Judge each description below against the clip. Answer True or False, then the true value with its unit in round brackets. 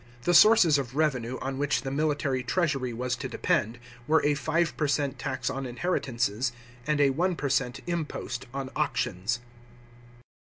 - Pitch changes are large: False (3.4 semitones)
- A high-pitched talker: False (135 Hz)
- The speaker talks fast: False (160 wpm)